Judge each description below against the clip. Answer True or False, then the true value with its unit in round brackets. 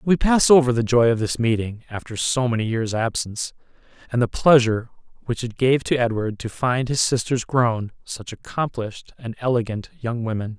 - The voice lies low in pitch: True (120 Hz)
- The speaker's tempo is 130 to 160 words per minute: False (180 wpm)